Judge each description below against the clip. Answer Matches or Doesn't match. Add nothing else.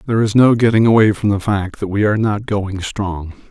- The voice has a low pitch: Matches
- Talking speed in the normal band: Doesn't match